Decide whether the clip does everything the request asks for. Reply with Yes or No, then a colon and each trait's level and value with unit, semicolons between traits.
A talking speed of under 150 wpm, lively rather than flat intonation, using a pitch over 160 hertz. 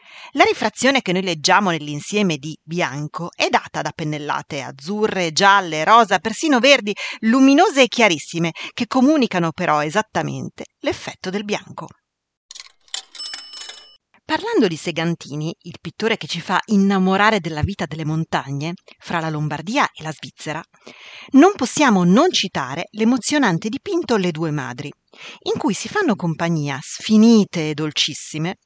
Yes: average, 130 wpm; wide, 5.9 semitones; medium, 185 Hz